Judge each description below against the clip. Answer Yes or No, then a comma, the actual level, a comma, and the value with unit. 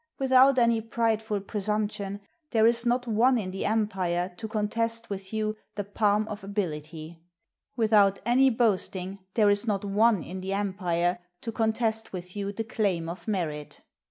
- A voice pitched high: Yes, high, 210 Hz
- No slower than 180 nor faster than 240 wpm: No, average, 160 wpm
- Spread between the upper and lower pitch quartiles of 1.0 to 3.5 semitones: Yes, average, 2.9 semitones